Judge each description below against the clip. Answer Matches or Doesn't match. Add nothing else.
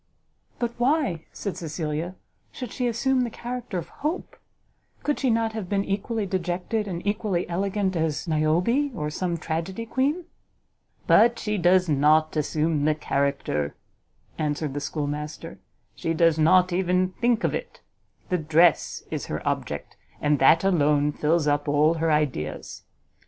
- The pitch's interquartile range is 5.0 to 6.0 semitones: Matches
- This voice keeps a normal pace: Matches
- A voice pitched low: Doesn't match